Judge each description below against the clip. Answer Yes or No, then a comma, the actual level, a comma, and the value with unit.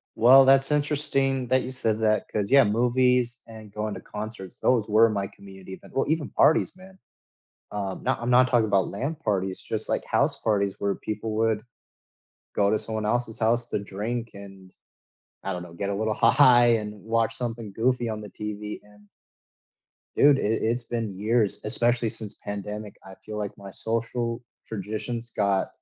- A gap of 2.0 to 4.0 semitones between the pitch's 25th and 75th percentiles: Yes, average, 2.9 semitones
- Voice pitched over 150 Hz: No, low, 110 Hz